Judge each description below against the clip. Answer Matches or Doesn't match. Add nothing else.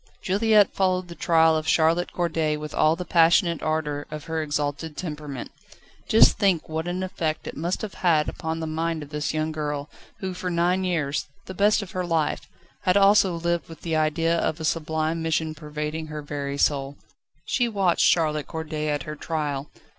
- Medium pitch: Matches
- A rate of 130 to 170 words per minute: Doesn't match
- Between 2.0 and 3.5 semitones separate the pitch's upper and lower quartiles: Matches